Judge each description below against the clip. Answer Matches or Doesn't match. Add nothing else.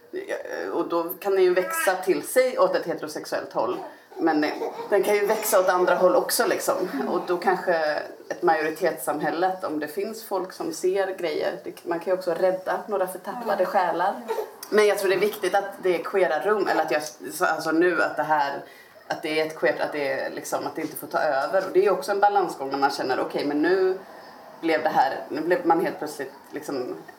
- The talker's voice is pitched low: Doesn't match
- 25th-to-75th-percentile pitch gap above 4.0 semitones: Doesn't match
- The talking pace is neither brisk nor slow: Doesn't match